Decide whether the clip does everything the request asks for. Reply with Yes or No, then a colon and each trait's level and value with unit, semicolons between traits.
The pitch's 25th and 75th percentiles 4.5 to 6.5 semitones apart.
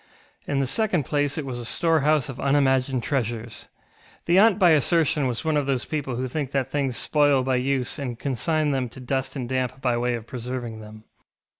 No: average, 2.9 semitones